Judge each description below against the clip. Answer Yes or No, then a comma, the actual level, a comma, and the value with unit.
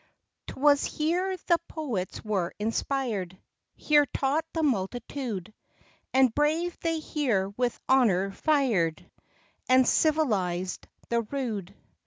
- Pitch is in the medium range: No, very high, 255 Hz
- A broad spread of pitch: Yes, wide, 7.0 semitones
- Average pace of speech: No, slow, 110 wpm